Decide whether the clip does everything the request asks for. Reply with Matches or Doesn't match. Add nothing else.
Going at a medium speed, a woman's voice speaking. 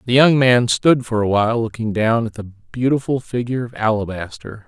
Doesn't match